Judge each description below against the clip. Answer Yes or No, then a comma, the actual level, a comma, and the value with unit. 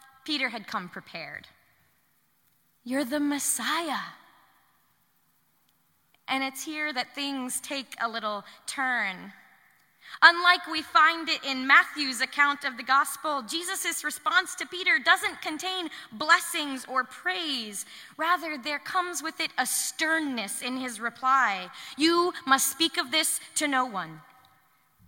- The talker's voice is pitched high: Yes, very high, 285 Hz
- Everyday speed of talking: No, slow, 125 wpm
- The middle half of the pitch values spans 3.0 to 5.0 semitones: Yes, average, 4.2 semitones